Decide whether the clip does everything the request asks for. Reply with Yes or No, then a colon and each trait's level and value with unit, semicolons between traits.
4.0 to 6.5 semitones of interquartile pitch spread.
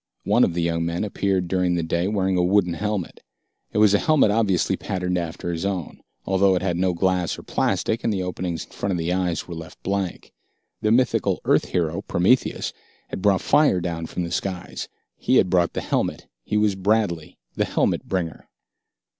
No: narrow, 2.5 semitones